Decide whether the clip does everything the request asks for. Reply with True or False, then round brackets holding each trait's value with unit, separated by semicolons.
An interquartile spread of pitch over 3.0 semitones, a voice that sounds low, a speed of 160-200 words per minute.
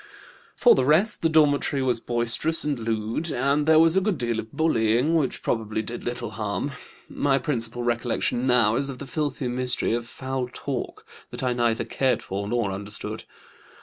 True (3.7 semitones; 125 Hz; 180 wpm)